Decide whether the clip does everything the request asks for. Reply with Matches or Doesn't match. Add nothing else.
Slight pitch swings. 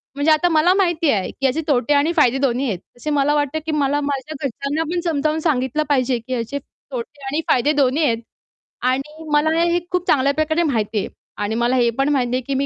Doesn't match